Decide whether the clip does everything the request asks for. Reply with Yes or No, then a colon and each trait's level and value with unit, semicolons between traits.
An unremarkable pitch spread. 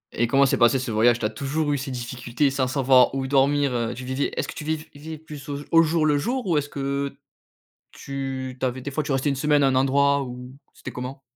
No: narrow, 2.2 semitones